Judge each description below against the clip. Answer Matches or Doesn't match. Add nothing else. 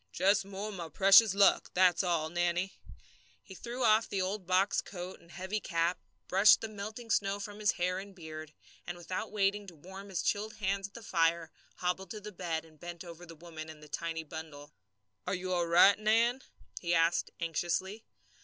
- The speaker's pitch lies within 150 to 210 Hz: Matches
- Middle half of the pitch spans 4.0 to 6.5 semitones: Doesn't match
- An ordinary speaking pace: Matches